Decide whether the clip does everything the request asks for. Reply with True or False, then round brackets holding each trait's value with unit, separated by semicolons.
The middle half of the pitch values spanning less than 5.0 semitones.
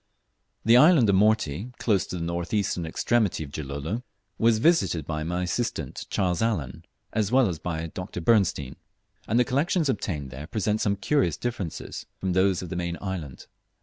False (5.5 semitones)